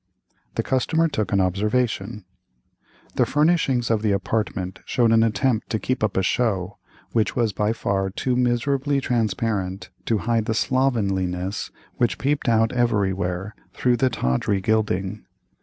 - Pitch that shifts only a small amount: No, average, 4.1 semitones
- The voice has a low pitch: Yes, low, 110 Hz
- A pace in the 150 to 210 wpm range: No, average, 140 wpm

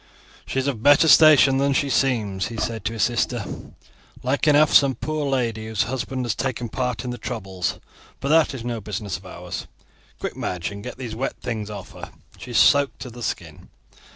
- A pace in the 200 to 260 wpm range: Yes, fast, 205 wpm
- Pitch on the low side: Yes, low, 125 Hz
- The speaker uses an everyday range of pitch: Yes, average, 3.8 semitones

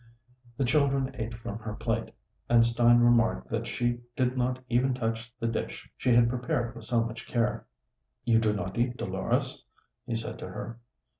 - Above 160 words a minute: Yes, average, 175 wpm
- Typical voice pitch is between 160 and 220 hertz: No, low, 120 Hz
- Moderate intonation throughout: No, narrow, 1.4 semitones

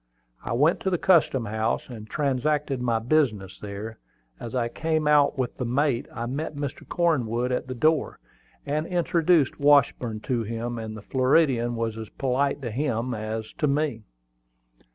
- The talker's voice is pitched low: Yes, low, 130 Hz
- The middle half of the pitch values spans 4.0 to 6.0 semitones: Yes, average, 4.5 semitones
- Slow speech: No, average, 165 wpm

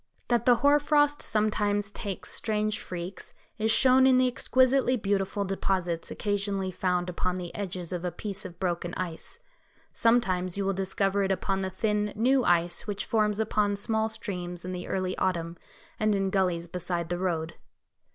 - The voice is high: Yes, high, 195 Hz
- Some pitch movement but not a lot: Yes, average, 3.1 semitones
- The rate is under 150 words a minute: No, average, 170 wpm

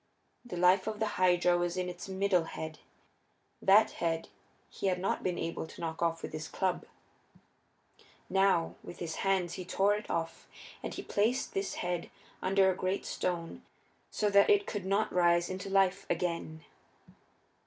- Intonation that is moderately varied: No, narrow, 2.3 semitones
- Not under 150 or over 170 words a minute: Yes, average, 165 wpm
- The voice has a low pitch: No, medium, 185 Hz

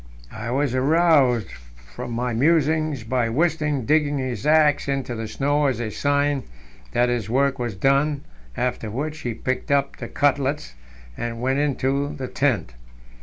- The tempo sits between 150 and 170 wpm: Yes, average, 155 wpm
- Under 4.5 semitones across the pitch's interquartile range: Yes, average, 3.3 semitones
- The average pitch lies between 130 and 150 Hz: Yes, low, 135 Hz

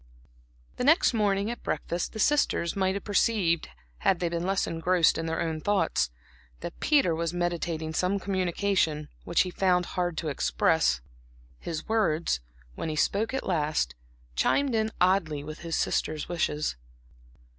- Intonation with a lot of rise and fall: No, average, 3.7 semitones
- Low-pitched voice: No, medium, 175 Hz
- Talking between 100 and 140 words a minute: No, average, 155 wpm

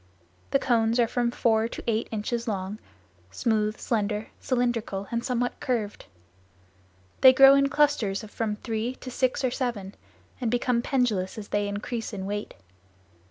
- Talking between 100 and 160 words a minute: Yes, average, 155 wpm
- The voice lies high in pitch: Yes, high, 230 Hz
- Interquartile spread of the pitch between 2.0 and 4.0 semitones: Yes, average, 2.9 semitones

